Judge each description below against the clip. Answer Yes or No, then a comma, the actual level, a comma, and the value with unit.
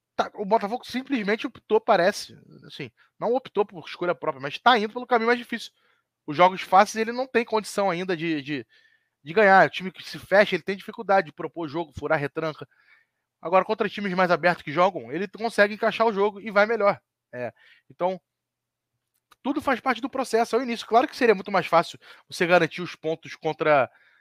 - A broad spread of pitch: Yes, wide, 6.2 semitones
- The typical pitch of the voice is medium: No, high, 195 Hz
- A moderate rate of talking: No, fast, 195 wpm